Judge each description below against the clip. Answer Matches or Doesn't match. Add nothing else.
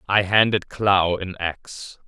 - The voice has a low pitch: Matches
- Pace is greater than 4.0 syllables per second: Doesn't match